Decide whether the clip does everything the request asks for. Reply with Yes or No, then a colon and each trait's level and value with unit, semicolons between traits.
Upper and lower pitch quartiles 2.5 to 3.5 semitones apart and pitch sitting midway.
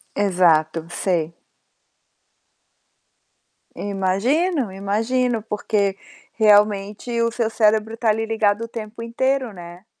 No: average, 3.0 semitones; high, 215 Hz